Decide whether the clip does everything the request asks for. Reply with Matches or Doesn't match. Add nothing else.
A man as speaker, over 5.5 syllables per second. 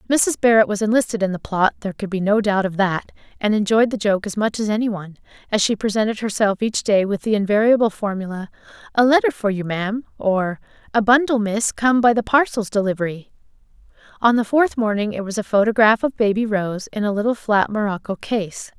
Doesn't match